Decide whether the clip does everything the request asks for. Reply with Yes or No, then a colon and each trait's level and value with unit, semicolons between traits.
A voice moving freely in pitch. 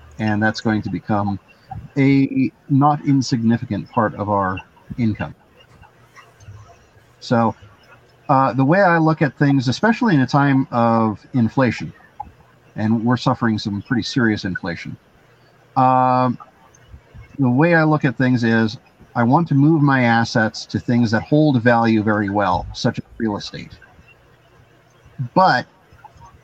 No: average, 3.8 semitones